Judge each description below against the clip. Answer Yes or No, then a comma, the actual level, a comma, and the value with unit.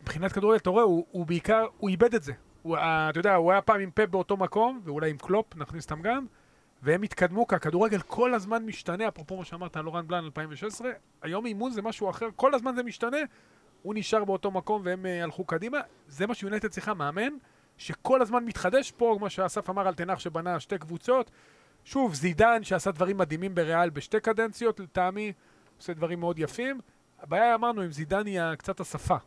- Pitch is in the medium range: No, high, 195 Hz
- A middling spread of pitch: Yes, average, 4.5 semitones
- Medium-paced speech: No, fast, 190 wpm